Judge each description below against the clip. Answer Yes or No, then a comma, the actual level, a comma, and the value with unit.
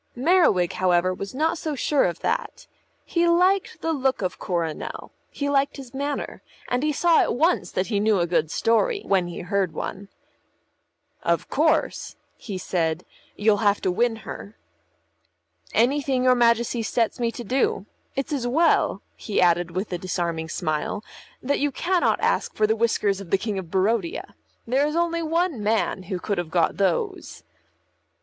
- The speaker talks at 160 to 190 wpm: Yes, average, 170 wpm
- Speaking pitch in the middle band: No, high, 220 Hz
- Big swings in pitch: Yes, wide, 7.3 semitones